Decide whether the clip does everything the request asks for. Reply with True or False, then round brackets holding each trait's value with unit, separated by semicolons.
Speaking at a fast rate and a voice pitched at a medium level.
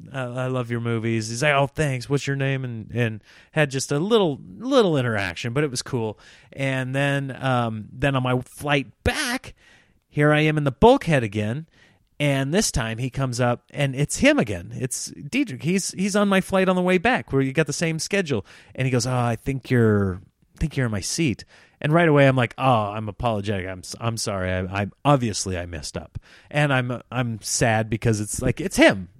False (215 wpm; 130 Hz)